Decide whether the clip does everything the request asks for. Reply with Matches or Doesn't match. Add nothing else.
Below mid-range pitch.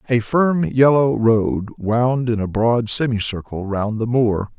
Matches